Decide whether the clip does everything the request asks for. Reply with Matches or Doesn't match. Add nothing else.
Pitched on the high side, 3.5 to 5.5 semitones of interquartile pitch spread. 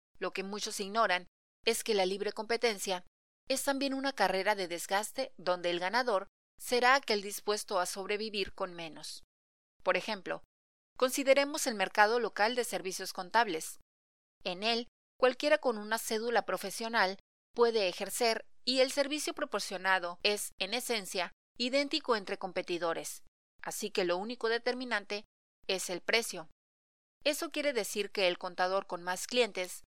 Matches